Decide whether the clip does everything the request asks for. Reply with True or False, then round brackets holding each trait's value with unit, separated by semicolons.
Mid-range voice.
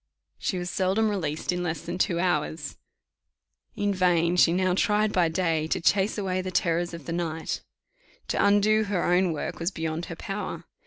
True (180 Hz)